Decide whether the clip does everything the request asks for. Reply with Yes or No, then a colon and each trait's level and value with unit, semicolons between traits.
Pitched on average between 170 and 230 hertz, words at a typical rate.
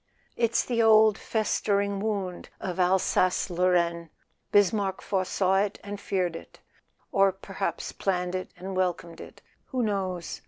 No: high, 190 Hz; slow, 125 wpm